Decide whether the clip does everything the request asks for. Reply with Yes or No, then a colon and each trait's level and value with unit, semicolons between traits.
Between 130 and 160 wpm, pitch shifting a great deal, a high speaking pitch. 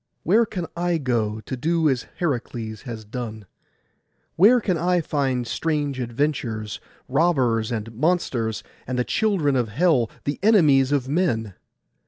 No: average, 140 wpm; wide, 6.4 semitones; low, 135 Hz